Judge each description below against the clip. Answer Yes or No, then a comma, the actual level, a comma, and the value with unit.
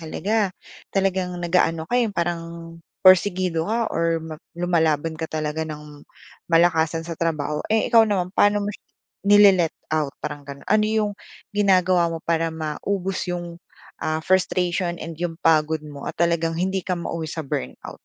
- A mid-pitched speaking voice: Yes, medium, 170 Hz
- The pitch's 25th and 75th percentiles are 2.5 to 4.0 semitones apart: Yes, average, 2.8 semitones